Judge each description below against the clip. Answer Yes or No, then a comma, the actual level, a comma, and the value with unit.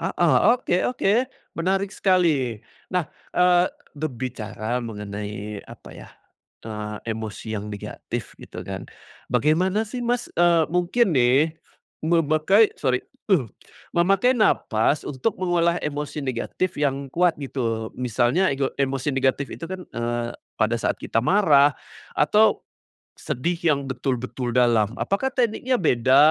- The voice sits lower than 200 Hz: Yes, medium, 140 Hz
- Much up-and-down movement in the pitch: Yes, wide, 6.9 semitones